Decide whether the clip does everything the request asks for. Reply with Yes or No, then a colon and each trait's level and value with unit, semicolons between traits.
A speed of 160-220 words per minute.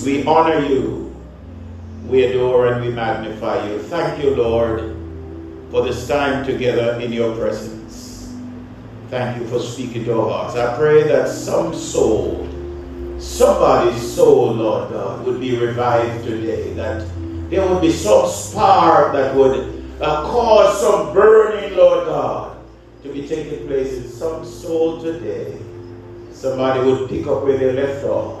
No: average, 150 wpm